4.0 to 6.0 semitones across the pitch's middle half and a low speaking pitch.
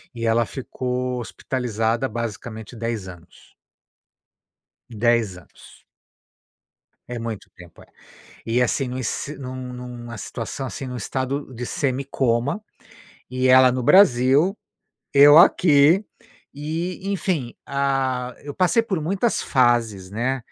No: average, 3.2 semitones; low, 125 Hz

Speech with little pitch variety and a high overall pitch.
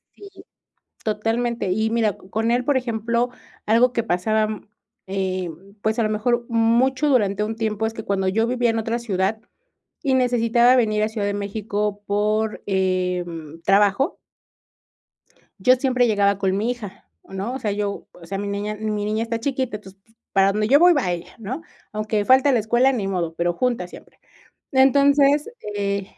No: average, 3.2 semitones; high, 215 Hz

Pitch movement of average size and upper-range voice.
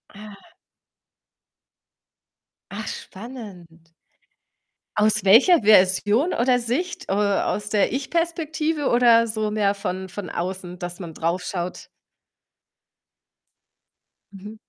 Yes: average, 4.6 semitones; high, 210 Hz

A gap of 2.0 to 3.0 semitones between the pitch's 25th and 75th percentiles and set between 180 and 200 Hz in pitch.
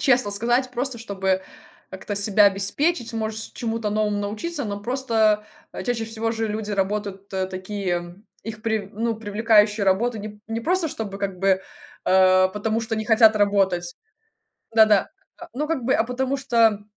No: narrow, 2.4 semitones; high, 215 Hz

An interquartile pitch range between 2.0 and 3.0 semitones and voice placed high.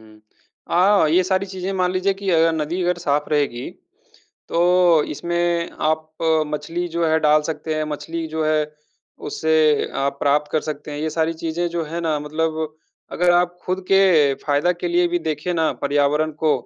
No: narrow, 2.5 semitones; medium, 160 Hz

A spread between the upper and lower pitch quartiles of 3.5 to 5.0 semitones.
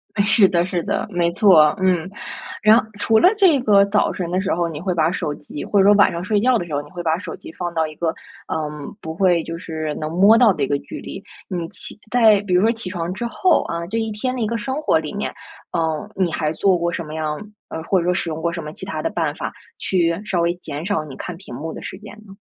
Yes: average, 4.2 semitones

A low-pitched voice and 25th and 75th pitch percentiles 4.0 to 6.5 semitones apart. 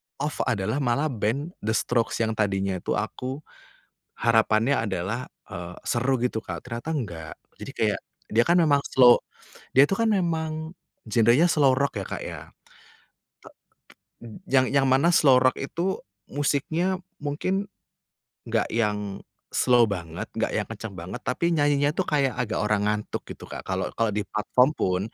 Yes: low, 125 Hz; wide, 5.4 semitones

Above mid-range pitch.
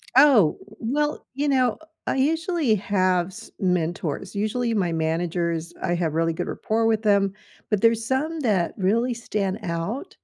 Yes: high, 210 Hz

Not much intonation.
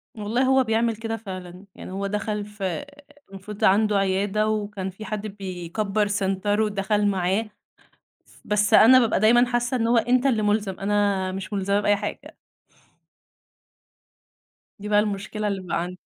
Yes: narrow, 2.0 semitones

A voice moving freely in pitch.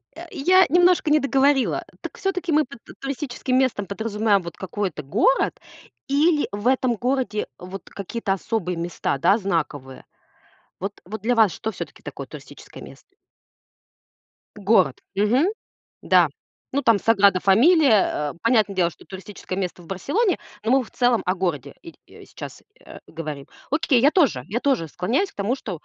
Yes: wide, 6.3 semitones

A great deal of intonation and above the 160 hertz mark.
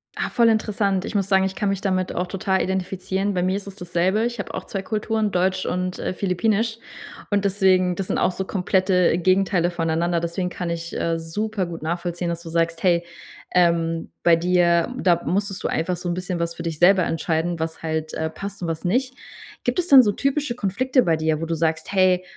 No: average, 2.7 semitones; medium, 185 Hz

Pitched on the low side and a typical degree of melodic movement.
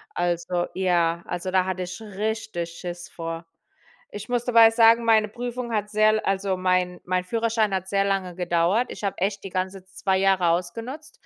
No: high, 190 Hz; average, 3.5 semitones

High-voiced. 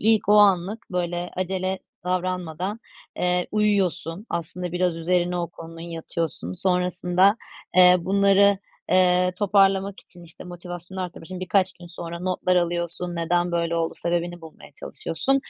No: medium, 180 Hz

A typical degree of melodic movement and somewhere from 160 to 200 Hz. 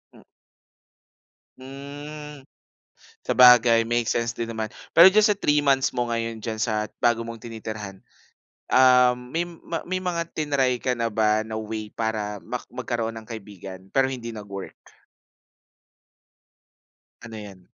No: average, 3.4 semitones; low, 115 Hz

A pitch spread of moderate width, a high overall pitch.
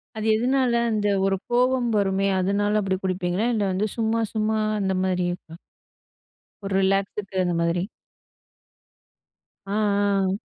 No: narrow, 2.2 semitones; high, 200 Hz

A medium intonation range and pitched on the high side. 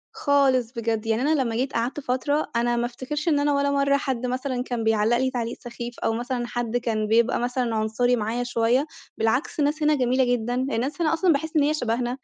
Yes: average, 3.1 semitones; high, 245 Hz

